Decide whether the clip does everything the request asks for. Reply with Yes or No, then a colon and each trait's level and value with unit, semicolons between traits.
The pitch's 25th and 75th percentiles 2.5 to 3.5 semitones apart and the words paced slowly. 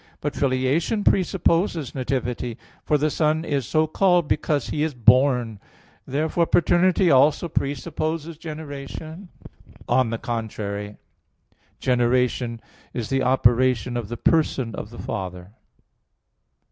No: average, 4.8 semitones; slow, 115 wpm